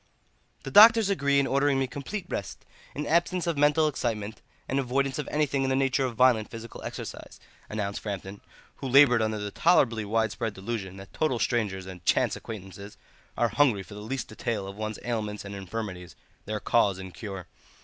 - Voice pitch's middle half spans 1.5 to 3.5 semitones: No, average, 5.1 semitones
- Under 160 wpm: No, average, 180 wpm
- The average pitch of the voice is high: No, low, 115 Hz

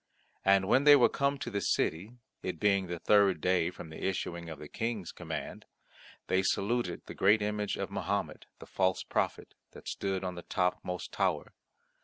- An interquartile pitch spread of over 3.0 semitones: No, narrow, 2.6 semitones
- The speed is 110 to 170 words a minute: No, average, 180 wpm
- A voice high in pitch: No, very low, 95 Hz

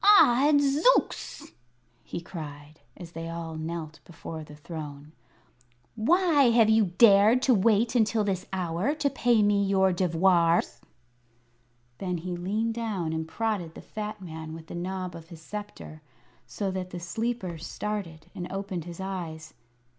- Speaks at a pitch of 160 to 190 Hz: Yes, medium, 185 Hz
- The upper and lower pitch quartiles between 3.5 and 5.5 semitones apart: Yes, average, 5.0 semitones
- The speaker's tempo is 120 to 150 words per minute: Yes, average, 145 wpm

